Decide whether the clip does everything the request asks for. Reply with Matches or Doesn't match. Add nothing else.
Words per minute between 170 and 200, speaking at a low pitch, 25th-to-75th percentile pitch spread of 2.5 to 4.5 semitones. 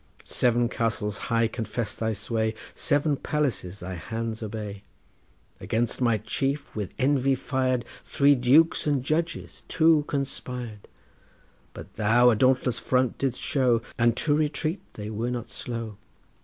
Doesn't match